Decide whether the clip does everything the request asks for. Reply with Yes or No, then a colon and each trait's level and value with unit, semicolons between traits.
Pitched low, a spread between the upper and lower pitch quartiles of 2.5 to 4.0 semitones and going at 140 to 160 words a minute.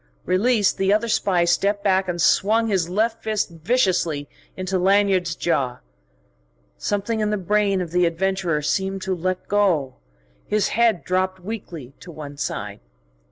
No: high, 190 Hz; average, 3.1 semitones; average, 150 wpm